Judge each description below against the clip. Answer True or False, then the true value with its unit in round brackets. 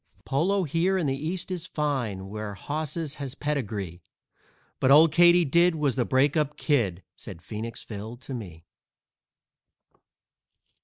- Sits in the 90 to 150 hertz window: True (140 Hz)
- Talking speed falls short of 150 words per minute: True (135 wpm)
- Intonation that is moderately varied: False (6.6 semitones)